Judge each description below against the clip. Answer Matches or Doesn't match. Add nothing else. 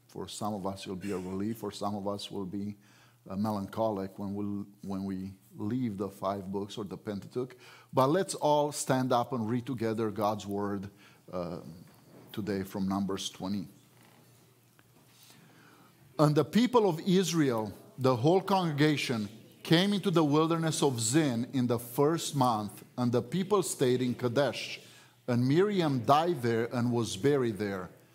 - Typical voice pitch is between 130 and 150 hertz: Doesn't match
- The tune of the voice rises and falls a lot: Matches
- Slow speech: Doesn't match